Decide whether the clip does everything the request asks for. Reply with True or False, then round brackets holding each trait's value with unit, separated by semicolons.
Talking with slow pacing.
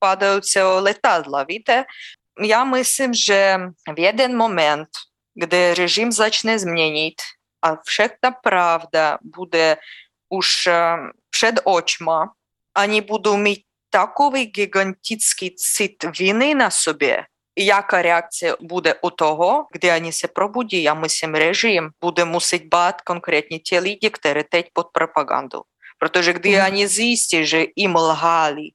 False (125 wpm)